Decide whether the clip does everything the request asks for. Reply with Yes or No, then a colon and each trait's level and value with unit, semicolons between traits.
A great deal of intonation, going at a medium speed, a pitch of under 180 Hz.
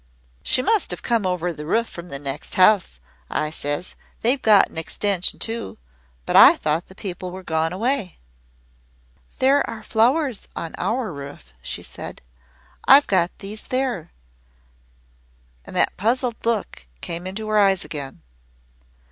No: wide, 5.8 semitones; average, 150 wpm; high, 195 Hz